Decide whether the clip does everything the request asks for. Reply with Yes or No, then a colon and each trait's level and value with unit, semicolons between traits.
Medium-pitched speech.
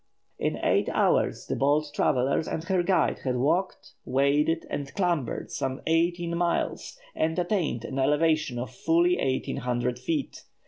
Yes: medium, 150 Hz